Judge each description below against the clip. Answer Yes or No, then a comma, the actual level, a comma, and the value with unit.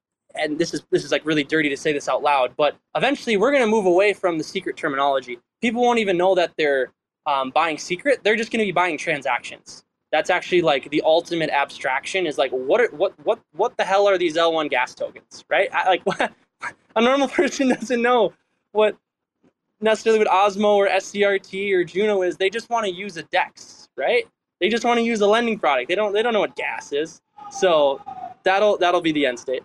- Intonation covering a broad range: Yes, wide, 6.0 semitones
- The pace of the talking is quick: Yes, fast, 220 wpm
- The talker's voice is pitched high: Yes, high, 200 Hz